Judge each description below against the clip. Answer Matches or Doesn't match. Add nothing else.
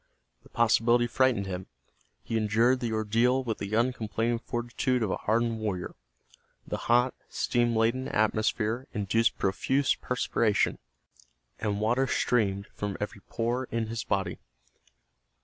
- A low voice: Matches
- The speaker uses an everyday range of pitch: Doesn't match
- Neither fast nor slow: Doesn't match